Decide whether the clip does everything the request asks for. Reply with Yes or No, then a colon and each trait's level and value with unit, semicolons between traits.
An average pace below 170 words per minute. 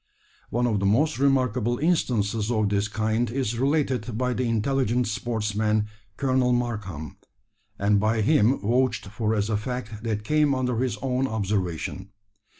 Yes: average, 150 wpm